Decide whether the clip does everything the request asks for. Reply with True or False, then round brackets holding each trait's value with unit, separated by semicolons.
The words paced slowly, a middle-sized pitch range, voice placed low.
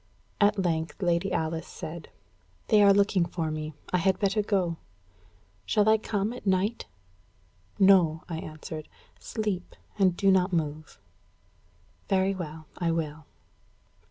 False (130 wpm; 3.6 semitones; 180 Hz)